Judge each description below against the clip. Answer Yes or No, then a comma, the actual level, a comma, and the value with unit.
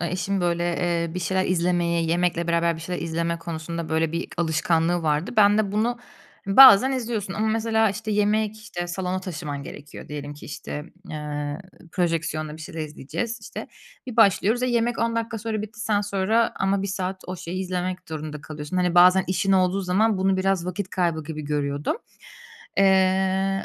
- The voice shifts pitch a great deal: No, average, 3.6 semitones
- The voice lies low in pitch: No, medium, 185 Hz